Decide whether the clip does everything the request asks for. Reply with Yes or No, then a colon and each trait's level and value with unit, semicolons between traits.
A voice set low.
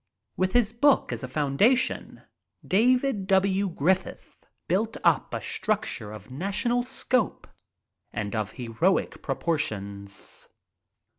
No: high, 190 Hz